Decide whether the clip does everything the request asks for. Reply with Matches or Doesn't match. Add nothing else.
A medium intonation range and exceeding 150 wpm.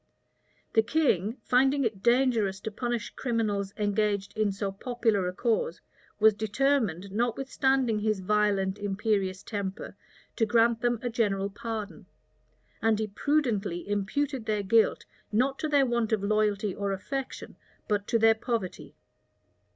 Doesn't match